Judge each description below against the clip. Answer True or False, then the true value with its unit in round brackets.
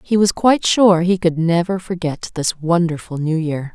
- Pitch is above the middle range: False (175 Hz)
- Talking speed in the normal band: True (190 wpm)